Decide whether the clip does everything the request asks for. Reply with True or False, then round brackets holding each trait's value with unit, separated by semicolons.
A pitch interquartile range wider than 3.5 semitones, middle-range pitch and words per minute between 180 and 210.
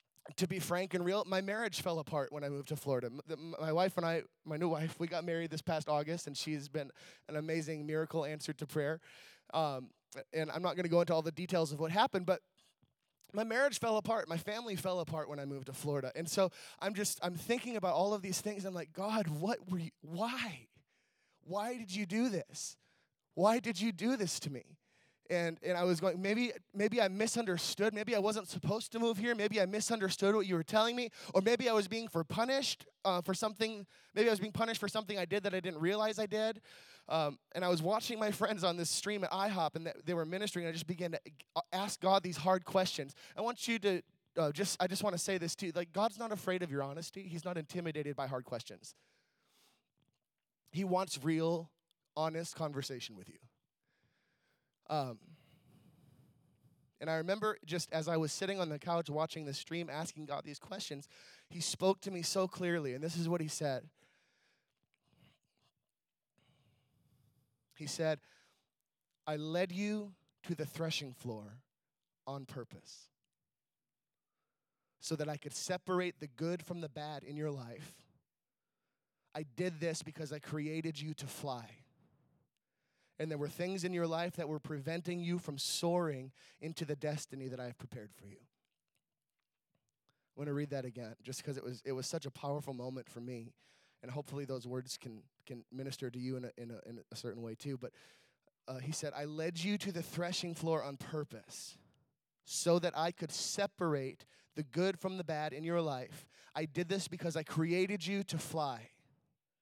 True (4.4 semitones; 165 Hz; 195 wpm)